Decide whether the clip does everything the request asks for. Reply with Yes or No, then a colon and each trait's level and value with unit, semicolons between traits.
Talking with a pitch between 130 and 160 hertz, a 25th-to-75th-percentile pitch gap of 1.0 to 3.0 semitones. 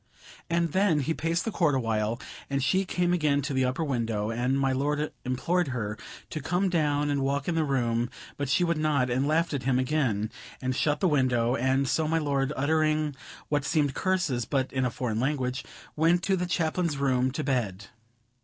No: medium, 140 Hz; average, 3.8 semitones